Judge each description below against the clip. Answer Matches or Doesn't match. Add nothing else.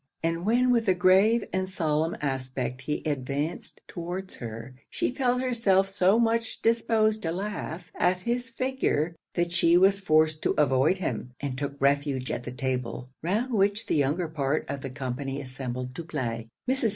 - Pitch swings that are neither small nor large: Doesn't match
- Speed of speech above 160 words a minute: Matches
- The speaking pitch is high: Doesn't match